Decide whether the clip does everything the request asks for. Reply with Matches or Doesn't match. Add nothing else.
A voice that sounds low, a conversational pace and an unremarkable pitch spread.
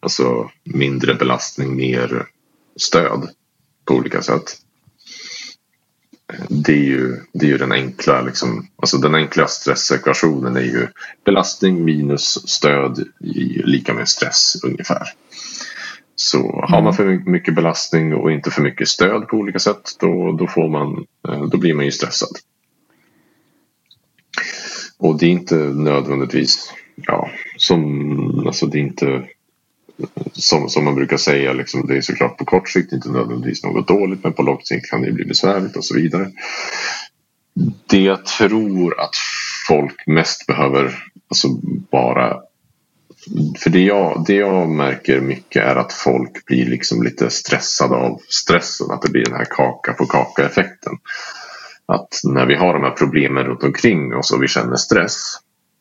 Matches